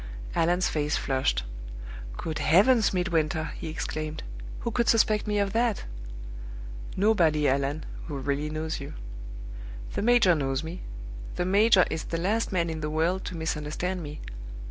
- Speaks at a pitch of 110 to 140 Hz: No, medium, 165 Hz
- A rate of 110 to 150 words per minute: Yes, average, 145 wpm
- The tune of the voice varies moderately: Yes, average, 4.3 semitones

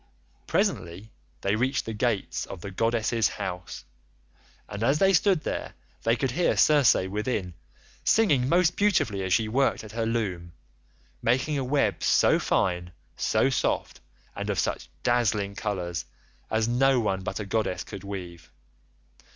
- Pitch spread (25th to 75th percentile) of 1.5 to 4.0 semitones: No, average, 5.3 semitones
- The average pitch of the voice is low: Yes, low, 110 Hz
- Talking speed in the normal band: Yes, average, 150 wpm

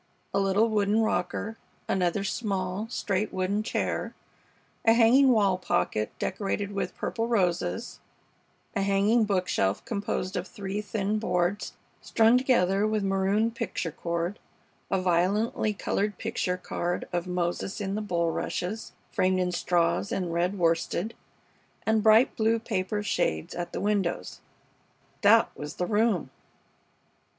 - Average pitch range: Yes, average, 3.2 semitones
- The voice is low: No, high, 195 Hz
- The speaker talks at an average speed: No, slow, 130 wpm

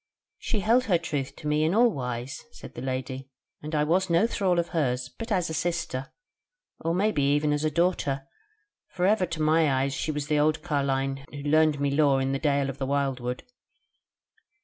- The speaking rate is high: Yes, fast, 210 wpm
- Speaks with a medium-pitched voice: Yes, medium, 150 Hz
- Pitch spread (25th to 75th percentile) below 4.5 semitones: Yes, average, 3.8 semitones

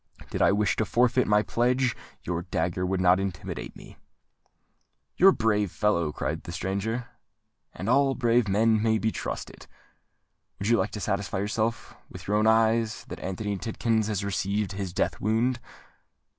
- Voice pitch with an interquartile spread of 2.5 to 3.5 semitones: Yes, average, 2.9 semitones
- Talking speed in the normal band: Yes, average, 170 wpm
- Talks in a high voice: No, low, 105 Hz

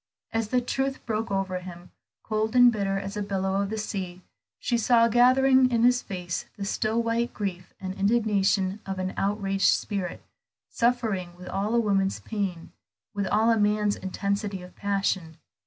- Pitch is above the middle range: Yes, high, 205 Hz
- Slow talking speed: No, average, 170 wpm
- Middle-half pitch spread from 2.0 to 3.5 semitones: Yes, average, 3.0 semitones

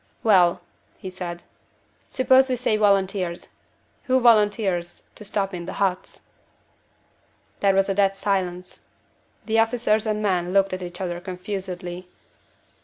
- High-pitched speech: Yes, high, 195 Hz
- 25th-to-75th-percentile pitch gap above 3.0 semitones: No, average, 2.7 semitones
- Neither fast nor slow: No, slow, 130 wpm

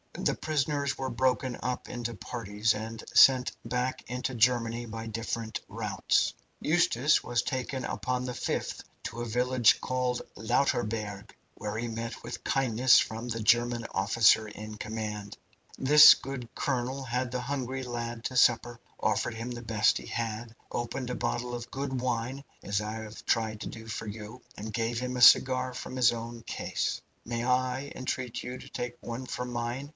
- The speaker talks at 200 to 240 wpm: No, average, 170 wpm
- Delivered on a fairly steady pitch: Yes, narrow, 2.1 semitones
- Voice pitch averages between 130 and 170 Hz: No, low, 120 Hz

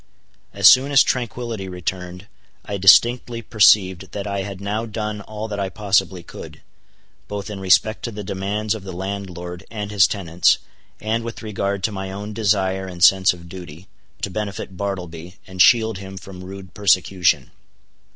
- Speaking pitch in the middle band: No, low, 100 Hz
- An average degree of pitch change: No, narrow, 2.2 semitones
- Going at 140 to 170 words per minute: Yes, average, 165 wpm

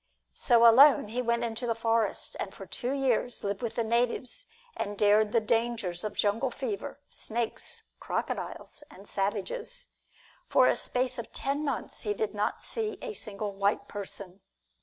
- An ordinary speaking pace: Yes, average, 160 wpm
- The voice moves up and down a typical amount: Yes, average, 3.4 semitones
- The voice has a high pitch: Yes, high, 230 Hz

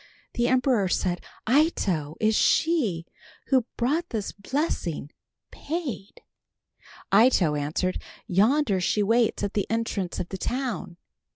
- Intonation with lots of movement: Yes, wide, 6.0 semitones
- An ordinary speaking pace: No, slow, 115 wpm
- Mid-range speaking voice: No, high, 215 Hz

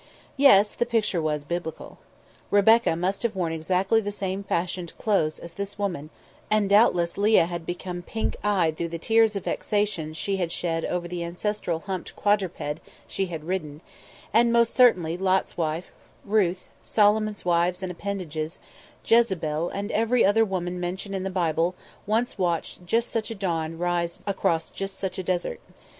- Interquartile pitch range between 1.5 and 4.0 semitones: Yes, average, 3.4 semitones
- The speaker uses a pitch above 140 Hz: Yes, medium, 185 Hz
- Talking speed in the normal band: Yes, average, 165 wpm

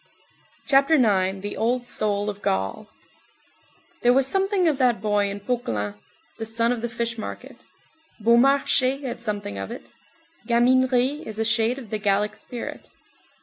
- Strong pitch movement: No, average, 3.6 semitones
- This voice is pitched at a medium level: No, high, 230 Hz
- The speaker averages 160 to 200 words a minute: No, average, 145 wpm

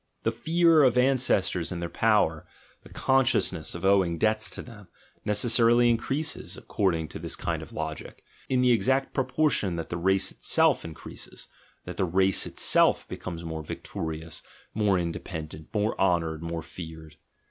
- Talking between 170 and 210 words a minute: No, average, 155 wpm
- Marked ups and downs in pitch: Yes, wide, 6.4 semitones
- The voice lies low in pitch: Yes, very low, 95 Hz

